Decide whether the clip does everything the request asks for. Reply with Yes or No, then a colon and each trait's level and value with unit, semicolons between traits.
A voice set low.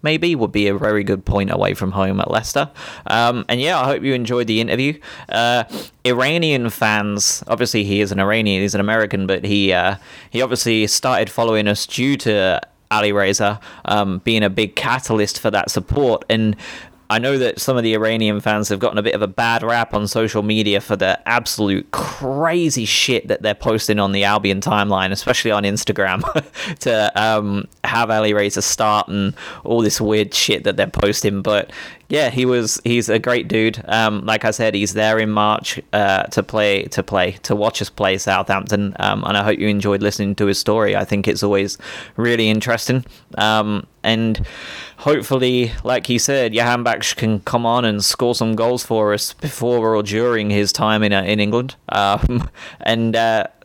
Yes: low, 110 Hz